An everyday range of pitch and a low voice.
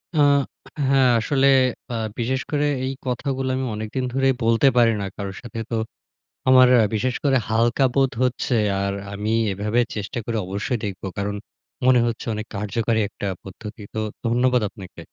Yes: average, 3.6 semitones; low, 115 Hz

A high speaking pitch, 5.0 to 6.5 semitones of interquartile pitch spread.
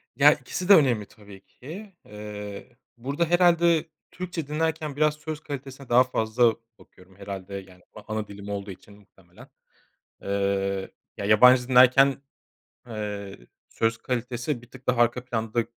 No: low, 120 Hz; wide, 5.5 semitones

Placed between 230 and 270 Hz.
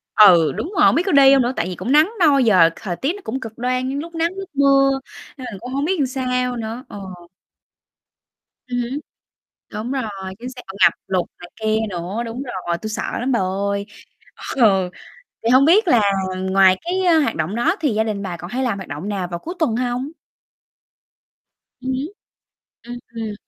Yes: high, 240 Hz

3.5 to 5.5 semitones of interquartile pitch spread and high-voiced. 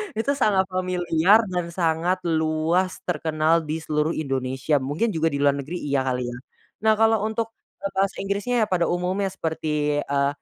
No: average, 4.2 semitones; medium, 170 Hz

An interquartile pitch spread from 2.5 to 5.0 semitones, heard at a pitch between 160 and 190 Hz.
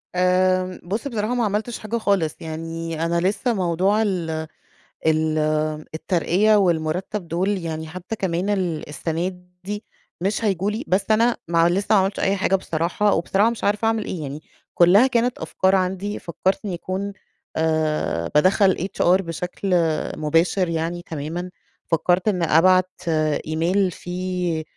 Yes: average, 3.3 semitones; medium, 185 Hz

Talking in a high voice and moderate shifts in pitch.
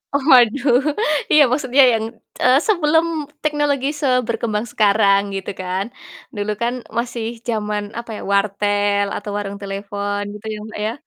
Yes: high, 220 Hz; average, 4.1 semitones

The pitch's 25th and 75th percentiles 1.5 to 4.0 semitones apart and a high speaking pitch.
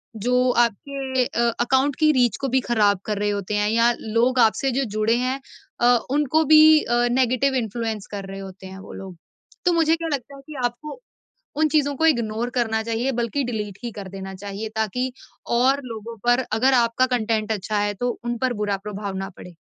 Yes: average, 3.7 semitones; high, 235 Hz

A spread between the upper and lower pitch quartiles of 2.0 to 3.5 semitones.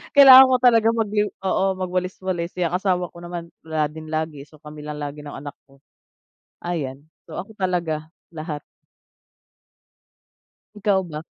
No: average, 3.9 semitones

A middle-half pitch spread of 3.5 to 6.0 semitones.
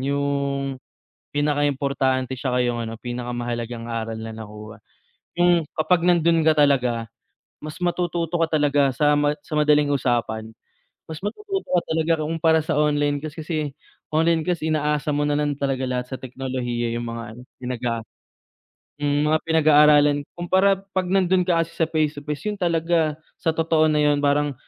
Yes: average, 3.9 semitones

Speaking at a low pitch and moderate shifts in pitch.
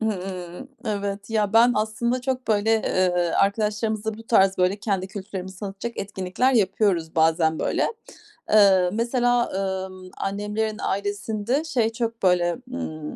No: high, 205 Hz; average, 3.1 semitones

